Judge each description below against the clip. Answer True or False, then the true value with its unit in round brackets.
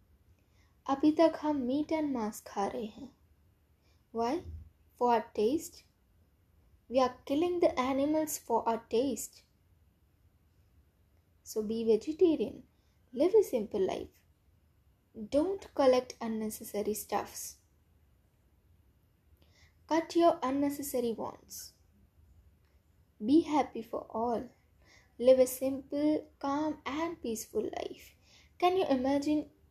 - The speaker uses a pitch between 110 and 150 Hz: False (230 Hz)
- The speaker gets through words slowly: True (100 wpm)